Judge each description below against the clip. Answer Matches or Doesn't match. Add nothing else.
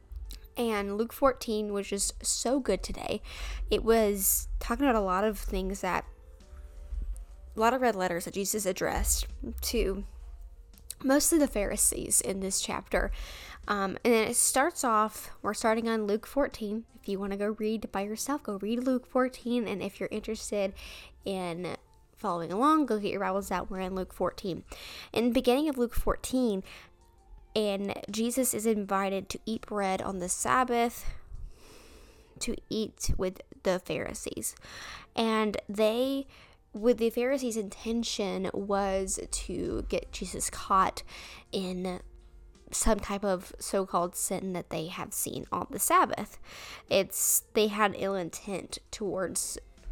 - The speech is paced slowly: Doesn't match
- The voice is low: Doesn't match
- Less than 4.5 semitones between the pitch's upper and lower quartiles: Matches